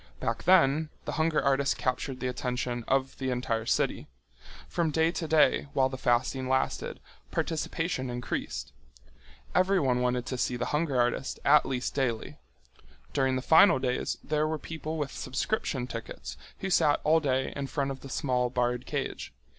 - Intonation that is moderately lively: Yes, average, 3.7 semitones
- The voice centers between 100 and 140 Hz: Yes, low, 135 Hz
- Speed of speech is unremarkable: Yes, average, 160 wpm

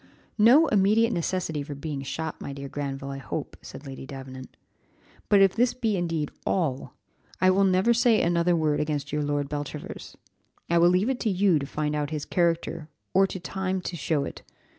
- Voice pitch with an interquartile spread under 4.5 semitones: No, average, 4.8 semitones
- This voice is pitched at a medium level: Yes, medium, 165 Hz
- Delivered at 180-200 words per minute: Yes, average, 190 wpm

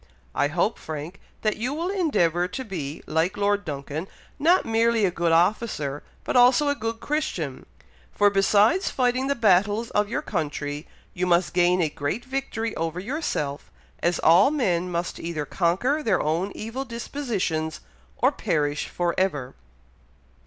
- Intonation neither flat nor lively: No, wide, 6.1 semitones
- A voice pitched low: No, high, 190 Hz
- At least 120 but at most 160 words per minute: Yes, average, 150 wpm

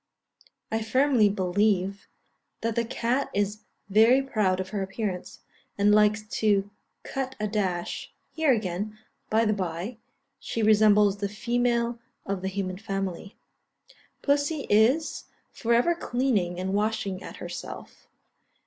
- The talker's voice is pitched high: Yes, high, 210 Hz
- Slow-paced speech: Yes, slow, 130 wpm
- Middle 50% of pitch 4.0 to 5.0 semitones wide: No, average, 3.2 semitones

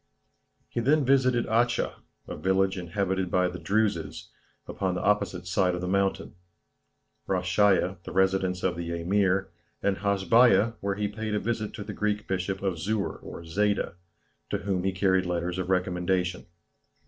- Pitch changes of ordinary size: No, narrow, 2.3 semitones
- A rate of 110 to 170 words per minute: Yes, average, 160 wpm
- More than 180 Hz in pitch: No, very low, 95 Hz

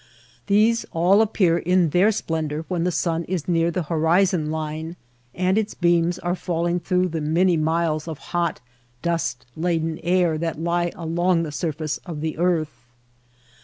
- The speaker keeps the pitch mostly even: Yes, narrow, 2.0 semitones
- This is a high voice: No, medium, 170 Hz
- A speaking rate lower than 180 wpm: Yes, average, 160 wpm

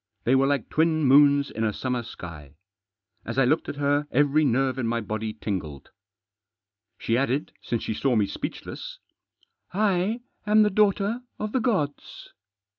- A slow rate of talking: No, average, 165 wpm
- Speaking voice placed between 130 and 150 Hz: Yes, medium, 140 Hz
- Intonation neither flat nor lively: No, wide, 6.0 semitones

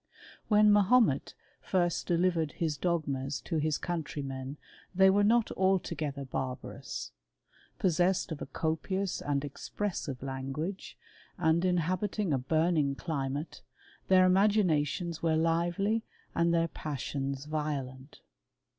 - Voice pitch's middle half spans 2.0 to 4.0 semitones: No, average, 4.6 semitones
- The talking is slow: Yes, slow, 110 wpm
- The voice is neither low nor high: Yes, medium, 165 Hz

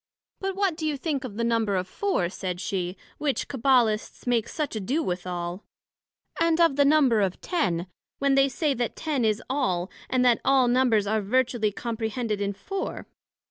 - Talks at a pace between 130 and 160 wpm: No, average, 180 wpm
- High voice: Yes, high, 240 Hz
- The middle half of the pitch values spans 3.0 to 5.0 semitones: No, wide, 5.5 semitones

